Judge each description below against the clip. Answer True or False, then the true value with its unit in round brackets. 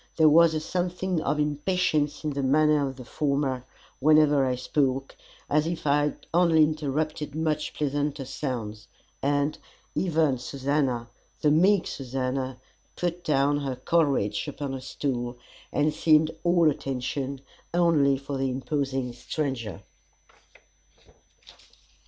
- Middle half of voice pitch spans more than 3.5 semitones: False (2.6 semitones)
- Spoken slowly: True (125 wpm)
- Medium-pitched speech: True (145 Hz)